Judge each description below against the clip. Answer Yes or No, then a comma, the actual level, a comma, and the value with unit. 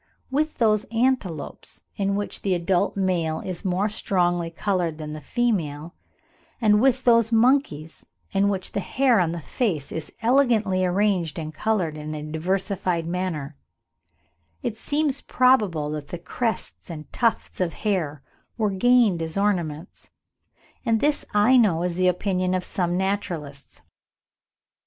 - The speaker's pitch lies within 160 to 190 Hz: Yes, medium, 185 Hz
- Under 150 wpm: Yes, average, 140 wpm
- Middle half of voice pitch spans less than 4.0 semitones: No, average, 4.9 semitones